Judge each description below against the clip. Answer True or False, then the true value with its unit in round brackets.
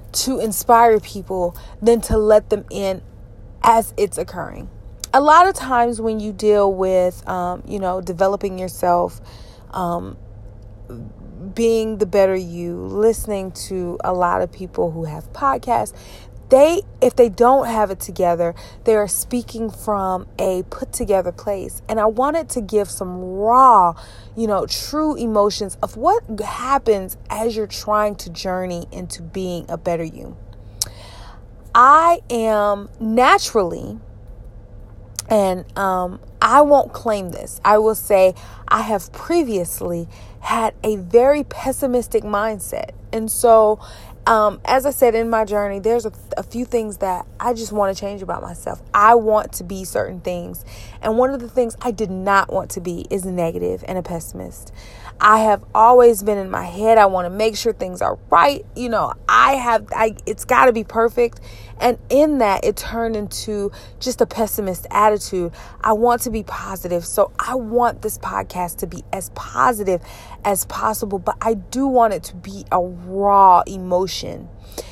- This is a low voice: False (205 Hz)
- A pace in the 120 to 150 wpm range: False (160 wpm)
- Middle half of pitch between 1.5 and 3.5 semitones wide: False (4.3 semitones)